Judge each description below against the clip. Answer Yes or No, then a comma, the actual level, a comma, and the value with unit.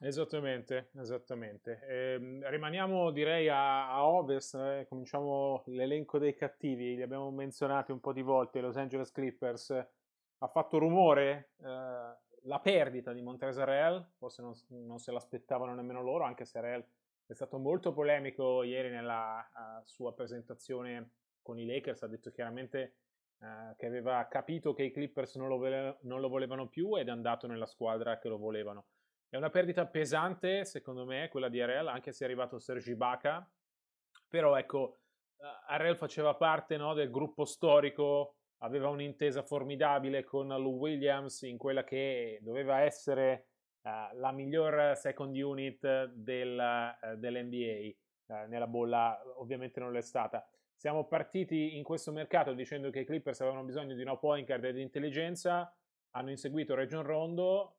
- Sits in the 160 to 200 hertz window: No, low, 135 Hz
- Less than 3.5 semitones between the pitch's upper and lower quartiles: Yes, average, 2.9 semitones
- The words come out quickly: No, average, 155 wpm